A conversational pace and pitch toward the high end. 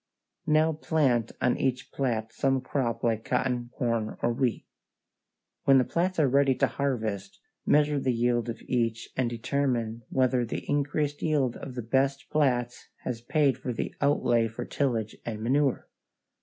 No: average, 155 wpm; low, 125 Hz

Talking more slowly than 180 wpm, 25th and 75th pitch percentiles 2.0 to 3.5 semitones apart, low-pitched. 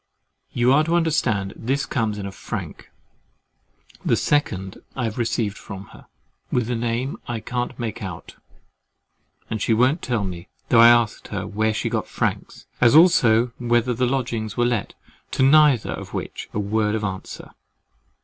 Yes: average, 170 wpm; average, 3.0 semitones; low, 115 Hz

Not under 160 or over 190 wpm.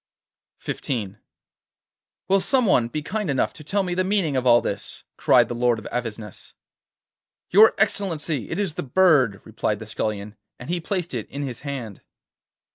Yes: average, 170 wpm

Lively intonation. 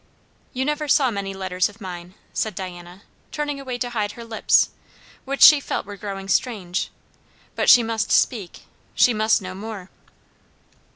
No: average, 4.5 semitones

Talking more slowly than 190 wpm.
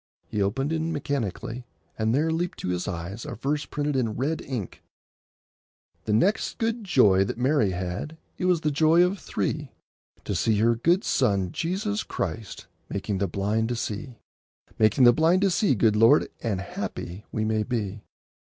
Yes: average, 170 wpm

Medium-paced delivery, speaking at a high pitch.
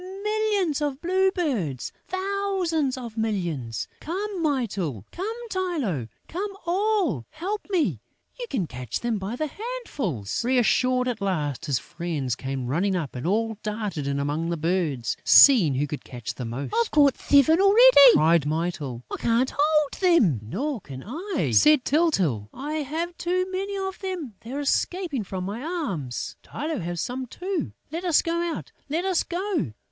Yes: average, 160 wpm; very high, 255 Hz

